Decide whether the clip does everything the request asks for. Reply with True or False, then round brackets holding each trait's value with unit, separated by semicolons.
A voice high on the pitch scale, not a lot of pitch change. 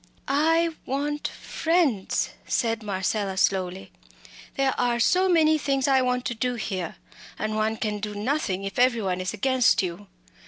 False (235 Hz; 5.5 semitones)